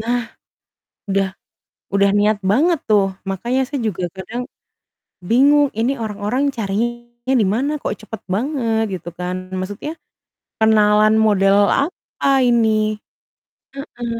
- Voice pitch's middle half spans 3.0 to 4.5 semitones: Yes, average, 3.6 semitones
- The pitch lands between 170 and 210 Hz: No, high, 225 Hz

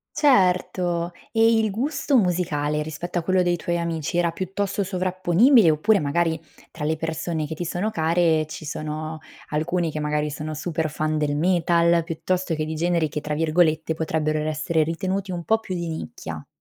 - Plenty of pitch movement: No, average, 2.7 semitones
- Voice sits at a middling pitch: Yes, medium, 170 Hz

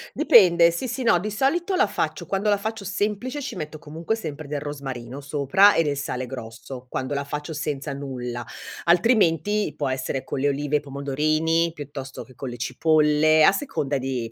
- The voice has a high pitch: No, medium, 150 Hz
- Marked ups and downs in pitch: Yes, wide, 5.9 semitones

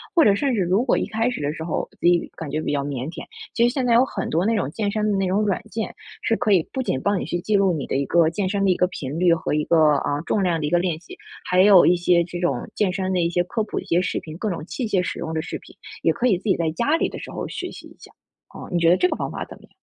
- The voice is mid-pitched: Yes, medium, 180 Hz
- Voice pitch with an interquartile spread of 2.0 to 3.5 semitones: No, average, 4.1 semitones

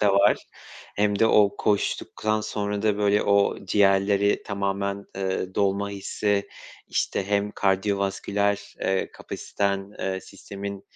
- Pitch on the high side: No, low, 100 Hz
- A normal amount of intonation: No, narrow, 0.8 semitones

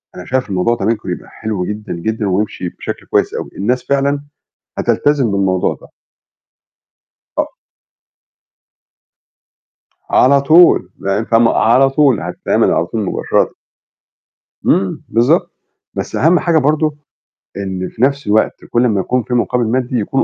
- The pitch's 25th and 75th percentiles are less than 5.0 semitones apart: No, average, 5.3 semitones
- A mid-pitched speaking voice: No, low, 115 Hz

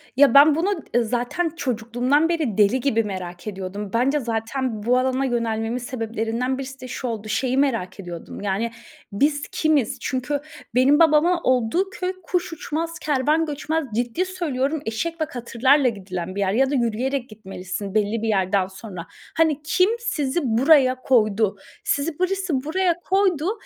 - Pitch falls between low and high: No, very high, 255 Hz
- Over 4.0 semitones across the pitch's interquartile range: Yes, wide, 5.6 semitones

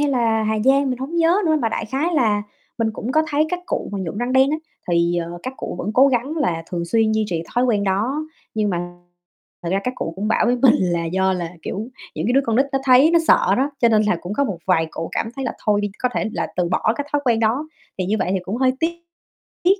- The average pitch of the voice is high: Yes, high, 225 Hz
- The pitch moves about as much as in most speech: No, wide, 5.9 semitones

